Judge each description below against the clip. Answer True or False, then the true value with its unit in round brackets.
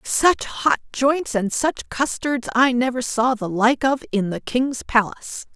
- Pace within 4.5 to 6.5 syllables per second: False (3.9 syllables/s)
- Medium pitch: False (250 Hz)